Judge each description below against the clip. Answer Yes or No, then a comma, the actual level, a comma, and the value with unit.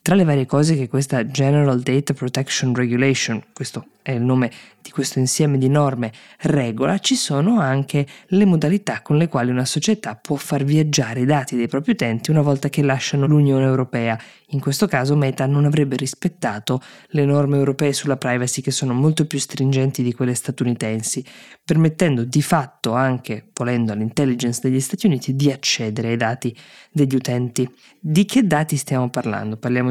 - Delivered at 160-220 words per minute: Yes, fast, 170 wpm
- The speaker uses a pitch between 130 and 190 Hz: Yes, low, 135 Hz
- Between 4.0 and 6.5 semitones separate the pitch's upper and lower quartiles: No, average, 2.8 semitones